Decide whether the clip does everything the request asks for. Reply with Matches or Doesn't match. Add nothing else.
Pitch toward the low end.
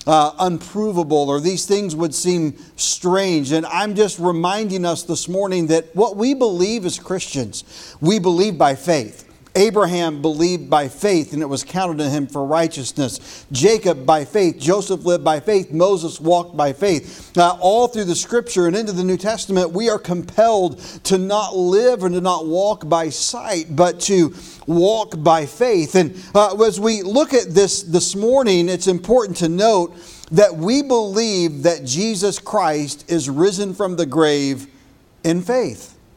Doesn't match